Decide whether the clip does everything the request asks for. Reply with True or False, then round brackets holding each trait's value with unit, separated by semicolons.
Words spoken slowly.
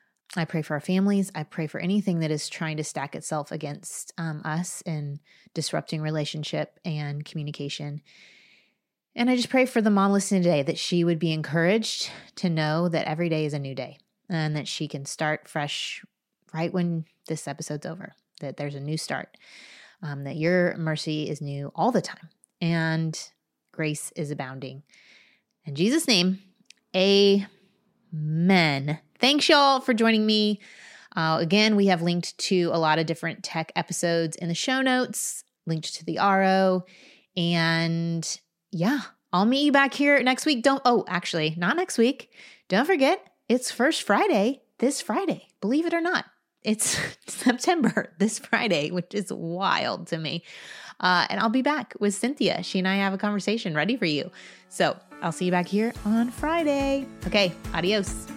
False (170 wpm)